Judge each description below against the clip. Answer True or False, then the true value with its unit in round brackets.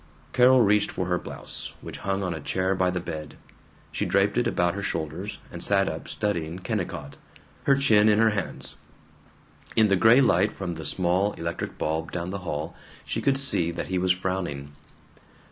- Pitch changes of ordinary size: True (3.5 semitones)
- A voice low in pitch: True (95 Hz)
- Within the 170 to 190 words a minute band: True (185 wpm)